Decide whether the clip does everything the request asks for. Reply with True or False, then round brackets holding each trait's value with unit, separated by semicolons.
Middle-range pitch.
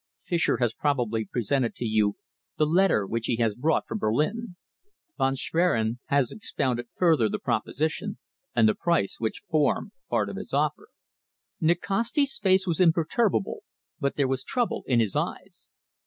True (145 Hz)